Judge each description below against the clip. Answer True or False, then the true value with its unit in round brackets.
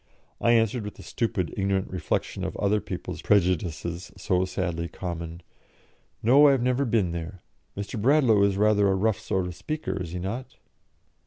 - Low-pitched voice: True (100 Hz)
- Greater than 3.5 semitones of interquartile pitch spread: True (3.9 semitones)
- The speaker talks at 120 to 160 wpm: False (170 wpm)